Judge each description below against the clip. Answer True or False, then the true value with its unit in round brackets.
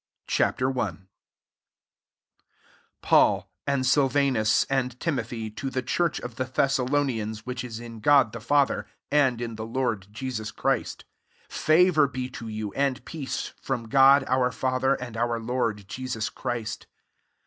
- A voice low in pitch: True (125 Hz)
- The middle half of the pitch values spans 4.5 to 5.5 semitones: False (3.0 semitones)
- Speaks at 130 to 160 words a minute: True (140 wpm)